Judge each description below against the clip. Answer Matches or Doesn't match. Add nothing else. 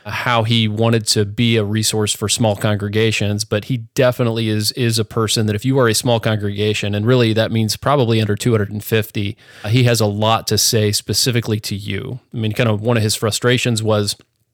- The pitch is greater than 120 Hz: Doesn't match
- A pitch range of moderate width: Doesn't match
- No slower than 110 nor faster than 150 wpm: Doesn't match